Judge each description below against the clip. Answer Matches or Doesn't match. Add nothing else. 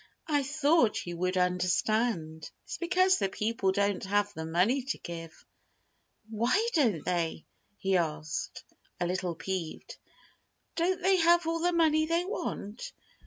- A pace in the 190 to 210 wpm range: Doesn't match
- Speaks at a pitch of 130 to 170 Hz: Doesn't match